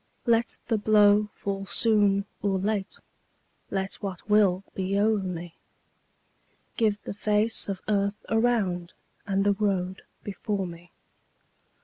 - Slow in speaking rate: Yes, slow, 120 wpm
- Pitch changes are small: Yes, narrow, 1.7 semitones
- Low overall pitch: No, high, 200 Hz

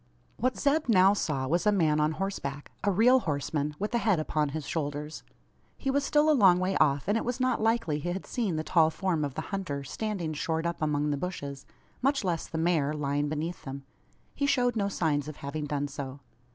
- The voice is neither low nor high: Yes, medium, 165 Hz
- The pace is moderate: No, fast, 220 wpm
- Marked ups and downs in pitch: Yes, wide, 6.0 semitones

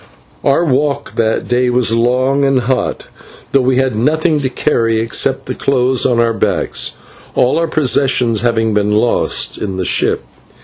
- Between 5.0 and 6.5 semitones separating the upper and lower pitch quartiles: No, average, 3.0 semitones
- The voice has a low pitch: Yes, low, 125 Hz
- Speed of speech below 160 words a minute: No, average, 165 wpm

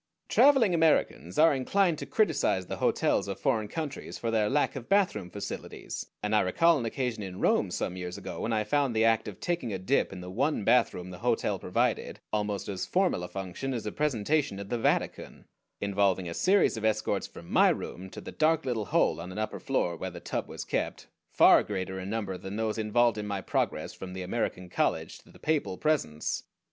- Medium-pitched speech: No, low, 110 Hz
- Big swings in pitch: Yes, wide, 6.5 semitones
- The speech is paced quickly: Yes, fast, 210 wpm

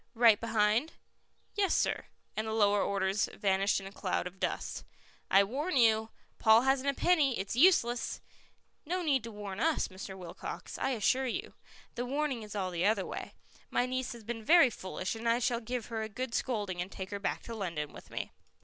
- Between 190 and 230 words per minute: Yes, average, 200 wpm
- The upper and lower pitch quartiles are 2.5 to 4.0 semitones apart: No, average, 4.4 semitones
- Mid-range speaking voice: No, high, 225 Hz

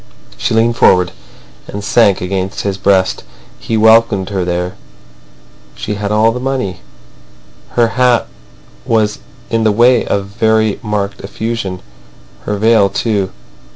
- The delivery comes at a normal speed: No, slow, 130 wpm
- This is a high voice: No, low, 105 Hz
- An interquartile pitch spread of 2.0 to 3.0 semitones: Yes, narrow, 2.6 semitones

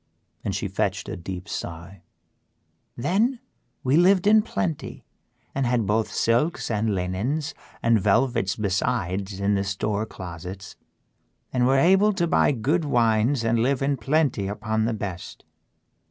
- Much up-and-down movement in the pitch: Yes, wide, 6.0 semitones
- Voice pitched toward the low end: Yes, low, 115 Hz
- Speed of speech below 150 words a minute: Yes, average, 140 wpm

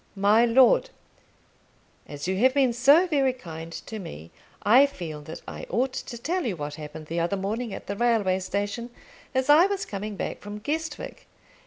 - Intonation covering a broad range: Yes, wide, 6.2 semitones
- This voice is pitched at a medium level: No, high, 220 Hz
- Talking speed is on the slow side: No, average, 180 wpm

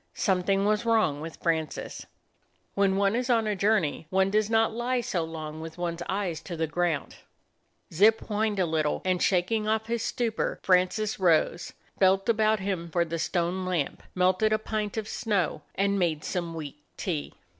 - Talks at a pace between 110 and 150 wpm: No, average, 175 wpm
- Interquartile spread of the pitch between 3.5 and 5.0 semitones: Yes, average, 4.3 semitones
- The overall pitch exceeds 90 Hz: Yes, high, 190 Hz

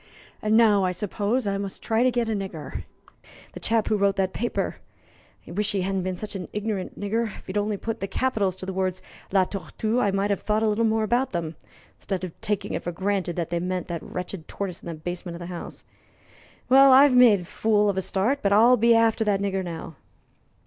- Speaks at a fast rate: Yes, fast, 230 wpm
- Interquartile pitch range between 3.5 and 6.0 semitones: No, average, 3.1 semitones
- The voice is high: Yes, high, 200 Hz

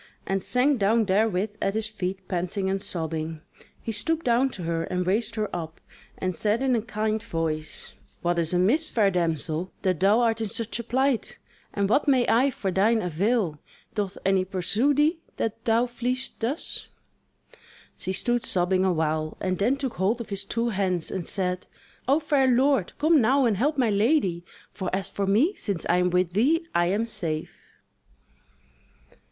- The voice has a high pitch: Yes, high, 205 Hz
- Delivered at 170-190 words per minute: Yes, average, 180 wpm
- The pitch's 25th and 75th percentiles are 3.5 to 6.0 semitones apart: Yes, average, 4.8 semitones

